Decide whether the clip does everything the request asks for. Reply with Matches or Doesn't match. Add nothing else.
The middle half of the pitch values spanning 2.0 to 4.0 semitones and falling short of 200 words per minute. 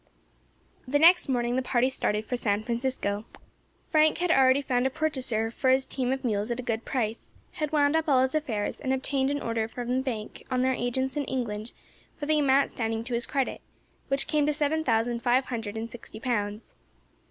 Doesn't match